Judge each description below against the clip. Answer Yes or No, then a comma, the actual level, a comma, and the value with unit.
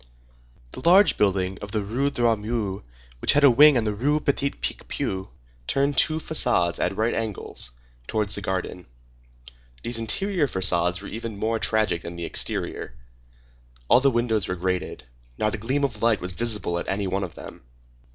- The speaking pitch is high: No, low, 110 Hz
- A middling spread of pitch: Yes, average, 4.7 semitones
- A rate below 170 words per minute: No, average, 175 wpm